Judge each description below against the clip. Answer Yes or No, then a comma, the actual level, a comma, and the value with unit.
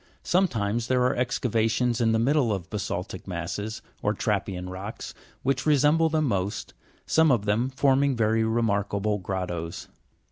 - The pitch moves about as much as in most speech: Yes, average, 4.5 semitones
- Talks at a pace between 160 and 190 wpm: No, average, 145 wpm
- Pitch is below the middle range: Yes, low, 115 Hz